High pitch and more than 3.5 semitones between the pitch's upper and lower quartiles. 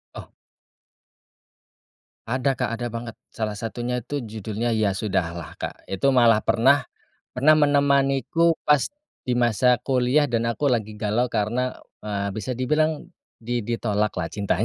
No: low, 120 Hz; average, 4.1 semitones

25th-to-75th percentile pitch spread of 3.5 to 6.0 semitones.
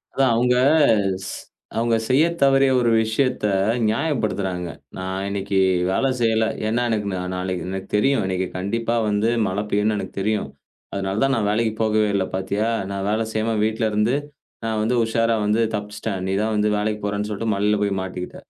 No: narrow, 2.5 semitones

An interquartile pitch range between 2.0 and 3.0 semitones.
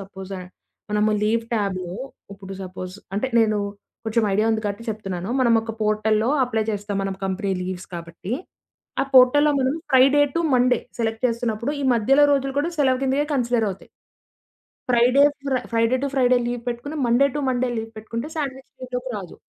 No: average, 3.8 semitones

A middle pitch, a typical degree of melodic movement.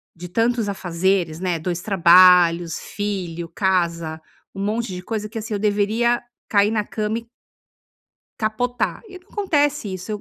No: high, 200 Hz; average, 4.0 semitones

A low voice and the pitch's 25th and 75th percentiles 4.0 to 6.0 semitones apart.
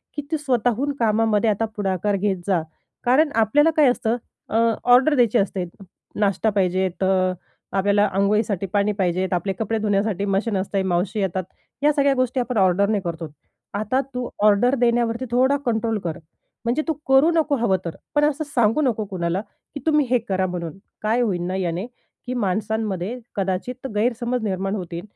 No: high, 210 Hz; average, 4.5 semitones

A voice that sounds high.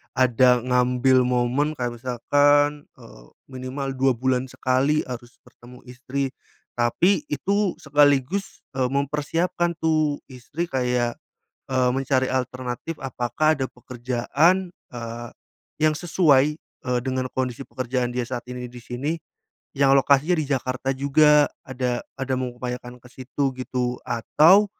No: low, 130 Hz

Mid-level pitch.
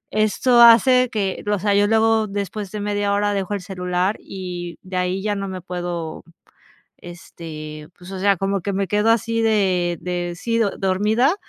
No: high, 195 Hz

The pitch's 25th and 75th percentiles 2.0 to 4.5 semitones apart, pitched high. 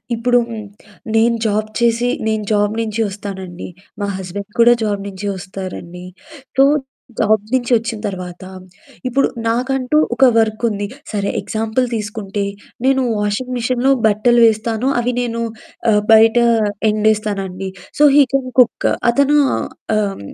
Yes: average, 2.9 semitones; high, 220 Hz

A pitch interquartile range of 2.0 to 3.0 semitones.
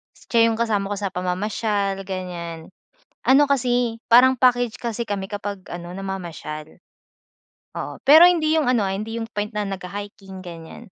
No: average, 3.8 semitones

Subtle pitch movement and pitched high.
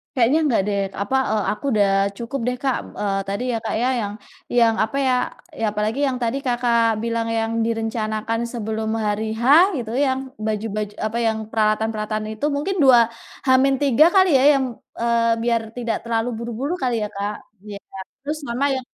No: average, 3.1 semitones; high, 230 Hz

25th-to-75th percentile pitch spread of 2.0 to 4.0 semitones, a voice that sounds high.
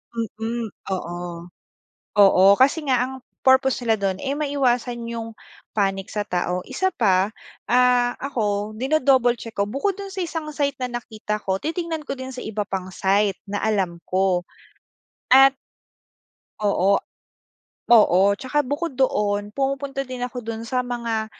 No: average, 4.7 semitones; high, 235 Hz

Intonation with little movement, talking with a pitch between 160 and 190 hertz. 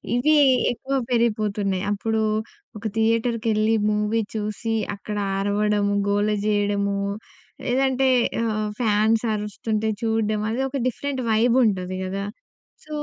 No: narrow, 1.9 semitones; high, 215 Hz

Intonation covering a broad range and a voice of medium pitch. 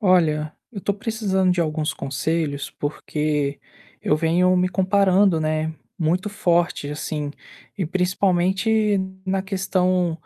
No: average, 3.5 semitones; medium, 180 Hz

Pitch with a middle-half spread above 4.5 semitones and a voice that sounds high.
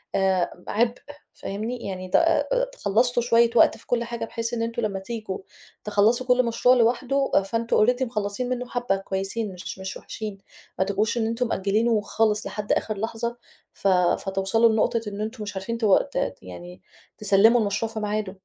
No: average, 3.1 semitones; high, 220 Hz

